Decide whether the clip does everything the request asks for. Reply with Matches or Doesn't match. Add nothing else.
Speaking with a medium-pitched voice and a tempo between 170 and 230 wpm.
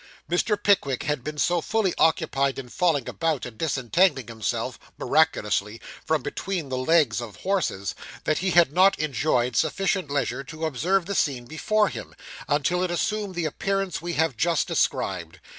Doesn't match